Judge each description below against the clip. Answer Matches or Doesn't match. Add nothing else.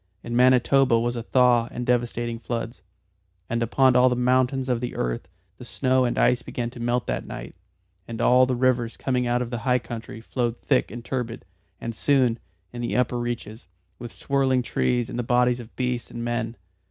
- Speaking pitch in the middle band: Doesn't match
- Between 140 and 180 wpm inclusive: Doesn't match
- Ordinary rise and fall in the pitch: Doesn't match